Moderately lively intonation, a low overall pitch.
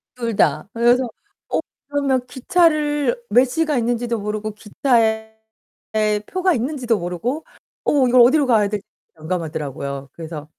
No: average, 4.9 semitones; high, 240 Hz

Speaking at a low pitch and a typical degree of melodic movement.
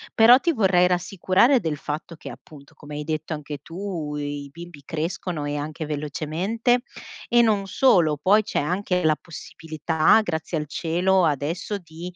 No: medium, 165 Hz; average, 4.1 semitones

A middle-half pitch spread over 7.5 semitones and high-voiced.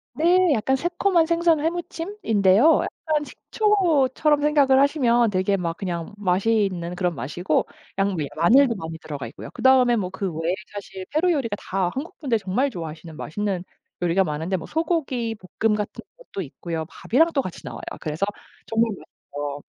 Yes: wide, 8.8 semitones; high, 220 Hz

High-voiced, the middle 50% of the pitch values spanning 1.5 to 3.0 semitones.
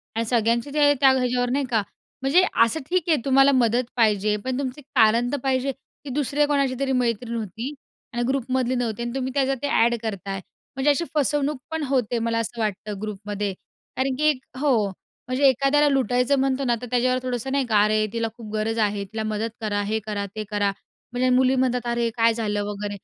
No: high, 245 Hz; average, 3.7 semitones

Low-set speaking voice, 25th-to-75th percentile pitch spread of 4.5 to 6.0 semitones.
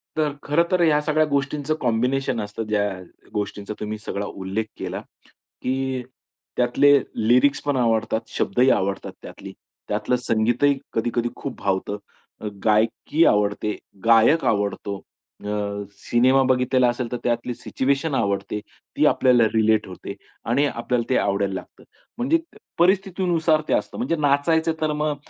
Yes: low, 125 Hz; average, 4.9 semitones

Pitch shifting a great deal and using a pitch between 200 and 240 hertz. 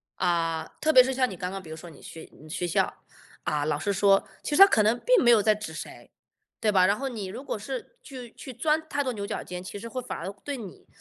Yes: wide, 6.1 semitones; high, 205 Hz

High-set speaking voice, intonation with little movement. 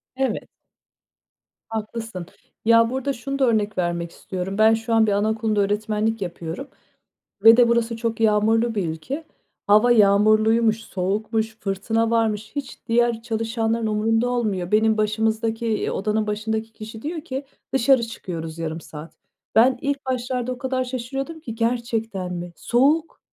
Yes: high, 225 Hz; narrow, 2.2 semitones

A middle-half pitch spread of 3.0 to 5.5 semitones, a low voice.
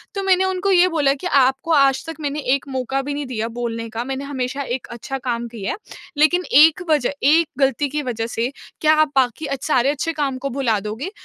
No: average, 3.7 semitones; very high, 275 Hz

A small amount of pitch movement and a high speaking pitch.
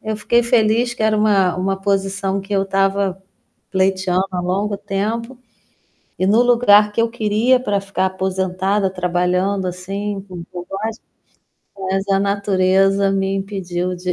Yes: narrow, 1.8 semitones; high, 195 Hz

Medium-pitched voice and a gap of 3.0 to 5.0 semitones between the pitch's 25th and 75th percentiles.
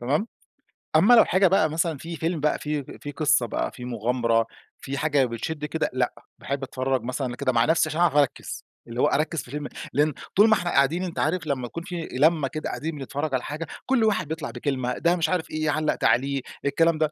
Yes: medium, 150 Hz; average, 3.7 semitones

